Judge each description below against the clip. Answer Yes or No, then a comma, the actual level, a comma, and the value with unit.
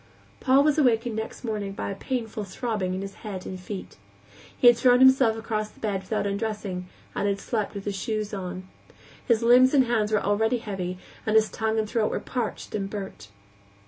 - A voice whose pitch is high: Yes, high, 215 Hz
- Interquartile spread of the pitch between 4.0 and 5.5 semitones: No, average, 2.8 semitones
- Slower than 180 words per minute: No, average, 200 wpm